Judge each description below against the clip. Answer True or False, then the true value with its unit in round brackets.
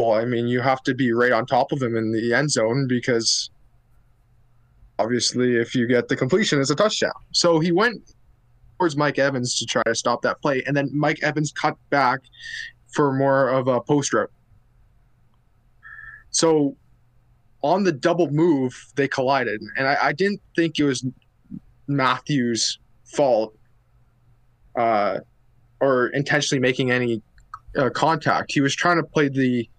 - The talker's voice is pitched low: True (125 Hz)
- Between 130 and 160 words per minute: True (155 wpm)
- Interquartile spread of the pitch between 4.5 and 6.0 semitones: False (3.6 semitones)